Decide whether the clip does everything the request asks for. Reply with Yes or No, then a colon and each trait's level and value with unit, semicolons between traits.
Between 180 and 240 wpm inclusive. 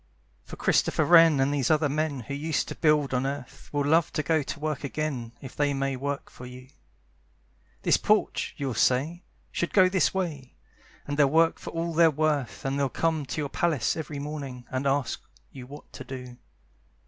Yes: average, 195 wpm